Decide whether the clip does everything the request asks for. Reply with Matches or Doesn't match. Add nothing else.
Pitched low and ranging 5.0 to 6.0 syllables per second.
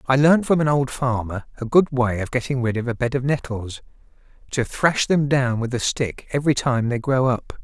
Matches